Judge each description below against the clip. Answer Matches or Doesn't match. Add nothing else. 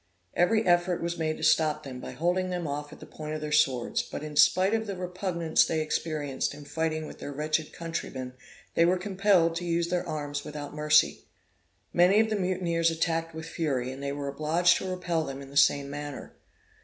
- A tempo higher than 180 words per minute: Matches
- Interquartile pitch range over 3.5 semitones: Doesn't match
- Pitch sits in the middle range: Matches